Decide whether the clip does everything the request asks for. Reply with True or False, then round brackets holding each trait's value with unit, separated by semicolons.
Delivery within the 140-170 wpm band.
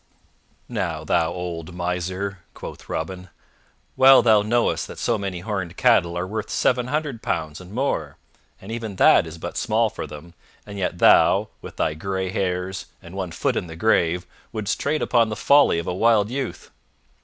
False (180 wpm)